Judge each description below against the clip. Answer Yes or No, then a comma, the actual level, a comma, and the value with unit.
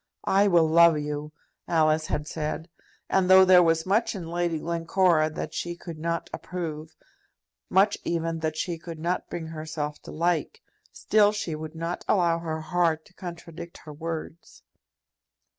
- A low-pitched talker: No, medium, 165 Hz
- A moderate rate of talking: Yes, average, 160 wpm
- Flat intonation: Yes, narrow, 1.9 semitones